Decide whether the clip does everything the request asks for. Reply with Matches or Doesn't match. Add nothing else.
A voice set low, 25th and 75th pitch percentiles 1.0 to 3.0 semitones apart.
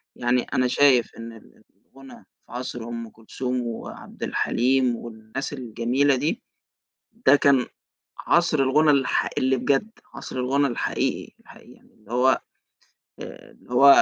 Matches